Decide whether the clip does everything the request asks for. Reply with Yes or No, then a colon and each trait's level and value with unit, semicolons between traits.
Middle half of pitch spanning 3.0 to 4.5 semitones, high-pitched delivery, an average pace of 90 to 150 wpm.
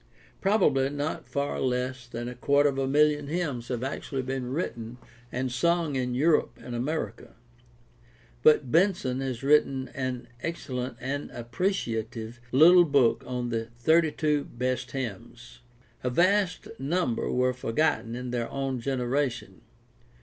No: average, 3.3 semitones; low, 130 Hz; average, 140 wpm